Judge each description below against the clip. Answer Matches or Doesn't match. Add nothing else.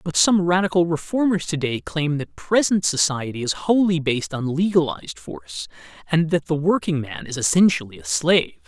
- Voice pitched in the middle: Matches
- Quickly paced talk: Doesn't match